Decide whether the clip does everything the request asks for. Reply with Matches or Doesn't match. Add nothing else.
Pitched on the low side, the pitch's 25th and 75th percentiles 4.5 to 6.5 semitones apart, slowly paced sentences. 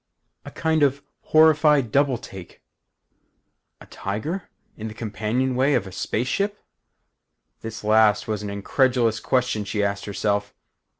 Matches